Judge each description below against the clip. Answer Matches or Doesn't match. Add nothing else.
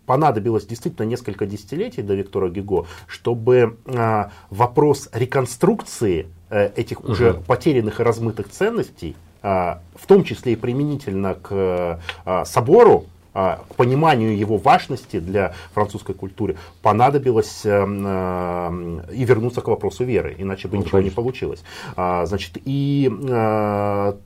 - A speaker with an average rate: Doesn't match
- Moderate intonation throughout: Matches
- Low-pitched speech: Matches